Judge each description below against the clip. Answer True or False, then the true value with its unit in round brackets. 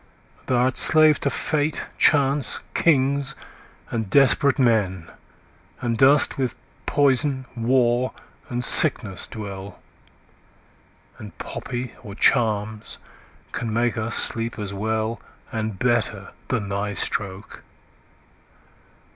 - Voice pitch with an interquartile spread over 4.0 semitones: False (3.7 semitones)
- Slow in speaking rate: True (105 wpm)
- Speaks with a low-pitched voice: True (120 Hz)